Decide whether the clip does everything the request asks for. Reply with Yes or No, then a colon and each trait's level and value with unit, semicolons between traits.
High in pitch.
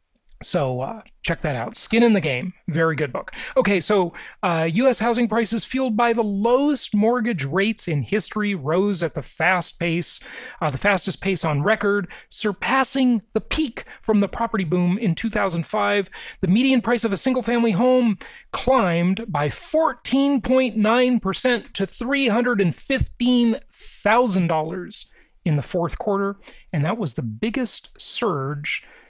Yes: high, 210 Hz